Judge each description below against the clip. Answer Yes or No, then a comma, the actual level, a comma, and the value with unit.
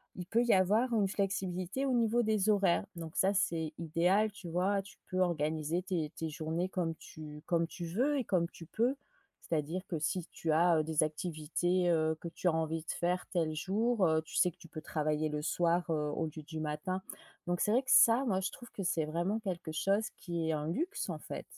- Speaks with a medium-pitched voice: Yes, medium, 175 Hz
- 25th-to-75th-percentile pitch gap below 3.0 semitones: No, average, 3.6 semitones